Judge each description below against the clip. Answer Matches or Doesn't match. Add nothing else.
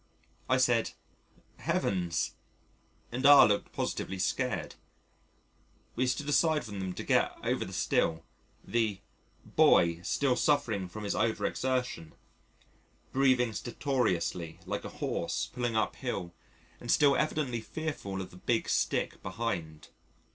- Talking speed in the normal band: Doesn't match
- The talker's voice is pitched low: Matches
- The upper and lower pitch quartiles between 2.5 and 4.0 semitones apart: Doesn't match